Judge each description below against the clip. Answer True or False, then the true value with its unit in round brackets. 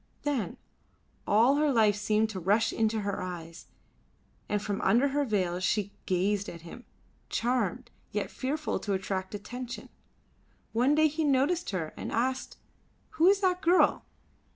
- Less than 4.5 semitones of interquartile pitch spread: False (5.6 semitones)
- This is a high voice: True (220 Hz)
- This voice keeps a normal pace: True (150 wpm)